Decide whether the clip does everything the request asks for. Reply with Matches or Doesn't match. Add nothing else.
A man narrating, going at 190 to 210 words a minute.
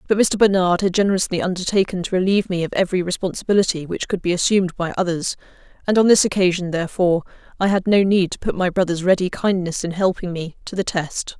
Doesn't match